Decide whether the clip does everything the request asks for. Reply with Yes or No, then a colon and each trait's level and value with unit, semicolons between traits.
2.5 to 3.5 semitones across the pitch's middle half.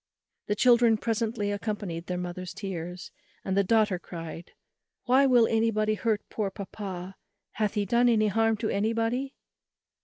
Yes: average, 3.1 semitones